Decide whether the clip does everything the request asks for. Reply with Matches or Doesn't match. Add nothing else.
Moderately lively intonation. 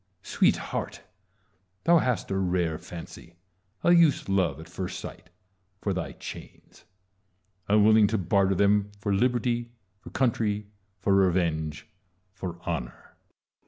Matches